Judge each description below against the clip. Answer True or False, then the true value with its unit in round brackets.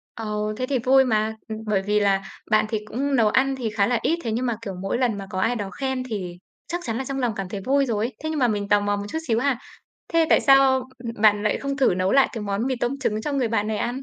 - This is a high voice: True (230 Hz)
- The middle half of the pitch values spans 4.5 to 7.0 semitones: False (4.0 semitones)